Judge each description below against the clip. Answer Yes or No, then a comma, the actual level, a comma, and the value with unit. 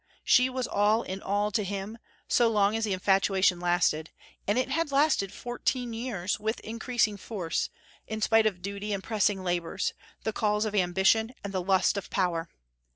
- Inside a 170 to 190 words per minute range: Yes, average, 175 wpm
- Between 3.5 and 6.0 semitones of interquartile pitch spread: No, average, 2.8 semitones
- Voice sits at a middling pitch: No, high, 205 Hz